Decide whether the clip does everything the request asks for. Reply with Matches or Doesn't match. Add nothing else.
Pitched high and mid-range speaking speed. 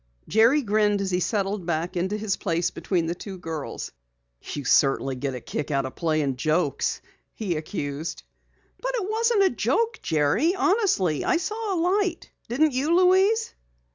Matches